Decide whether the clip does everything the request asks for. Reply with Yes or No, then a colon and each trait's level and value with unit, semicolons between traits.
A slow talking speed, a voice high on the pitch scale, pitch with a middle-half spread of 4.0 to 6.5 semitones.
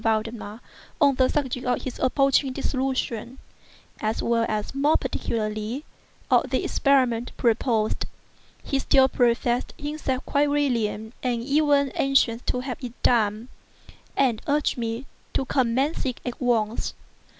No: slow, 130 wpm; very high, 250 Hz; average, 3.1 semitones